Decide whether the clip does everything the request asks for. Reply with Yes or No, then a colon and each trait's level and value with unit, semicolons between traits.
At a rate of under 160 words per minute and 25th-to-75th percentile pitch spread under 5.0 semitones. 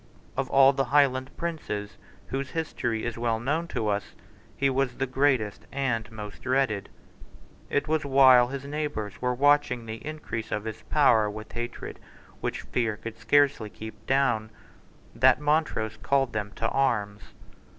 Yes: average, 150 wpm; average, 4.0 semitones